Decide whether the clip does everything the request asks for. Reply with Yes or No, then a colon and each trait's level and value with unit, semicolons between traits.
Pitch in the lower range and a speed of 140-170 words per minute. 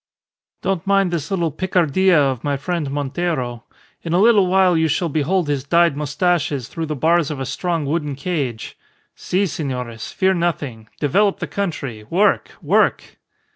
No: medium, 160 Hz; average, 160 wpm